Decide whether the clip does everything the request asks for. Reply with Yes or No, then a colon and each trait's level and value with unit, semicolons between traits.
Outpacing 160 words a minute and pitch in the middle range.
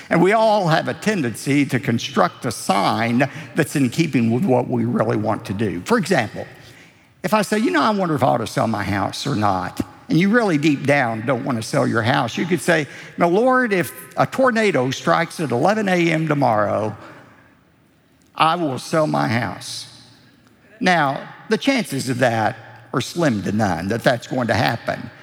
Yes: average, 195 wpm; medium, 160 Hz